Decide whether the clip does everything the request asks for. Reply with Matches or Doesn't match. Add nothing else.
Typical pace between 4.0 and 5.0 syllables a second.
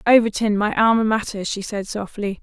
Doesn't match